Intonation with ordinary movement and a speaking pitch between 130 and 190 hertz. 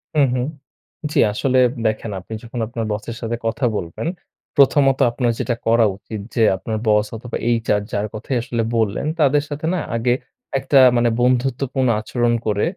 No: average, 3.1 semitones; low, 120 Hz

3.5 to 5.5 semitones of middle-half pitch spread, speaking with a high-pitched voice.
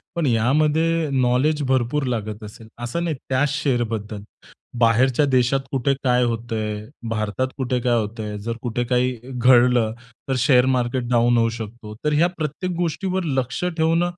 No: average, 4.0 semitones; low, 125 Hz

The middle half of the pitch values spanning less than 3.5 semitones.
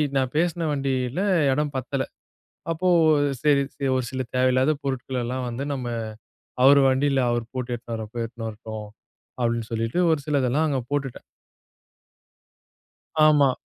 Yes: average, 2.9 semitones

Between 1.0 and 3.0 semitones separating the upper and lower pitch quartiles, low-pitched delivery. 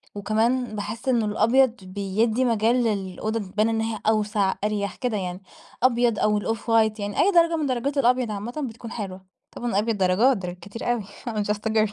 No: average, 2.7 semitones; high, 220 Hz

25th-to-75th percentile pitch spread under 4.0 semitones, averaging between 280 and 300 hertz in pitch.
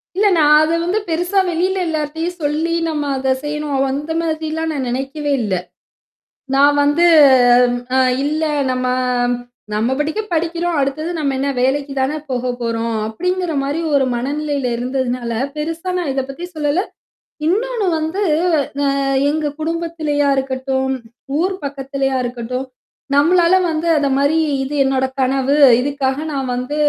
Yes: average, 3.4 semitones; very high, 290 Hz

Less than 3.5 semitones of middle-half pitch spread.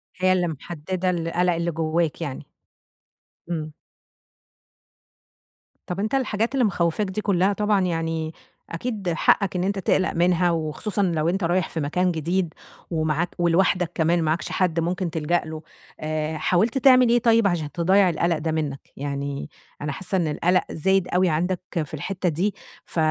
Yes: average, 2.9 semitones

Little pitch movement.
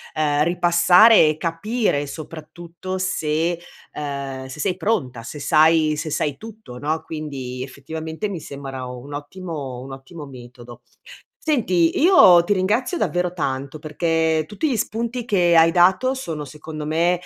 No: average, 4.2 semitones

